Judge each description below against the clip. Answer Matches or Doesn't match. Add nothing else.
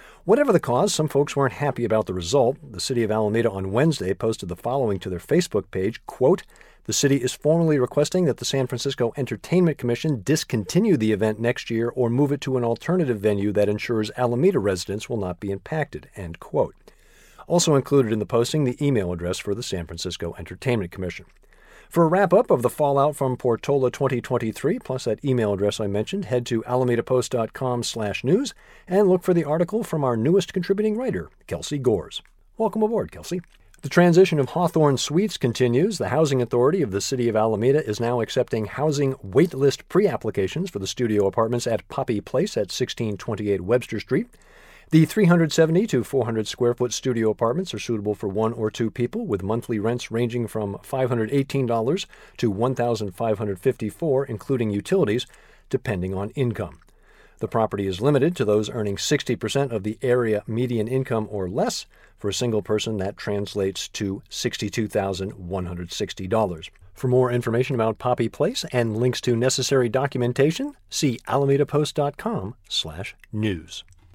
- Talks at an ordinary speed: Matches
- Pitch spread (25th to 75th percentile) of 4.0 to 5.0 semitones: Matches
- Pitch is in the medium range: Doesn't match